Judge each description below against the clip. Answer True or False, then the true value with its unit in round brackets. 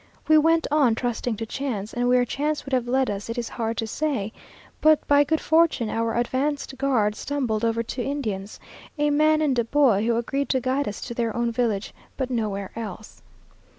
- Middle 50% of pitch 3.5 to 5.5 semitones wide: True (4.1 semitones)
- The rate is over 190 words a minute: True (200 wpm)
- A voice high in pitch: True (245 Hz)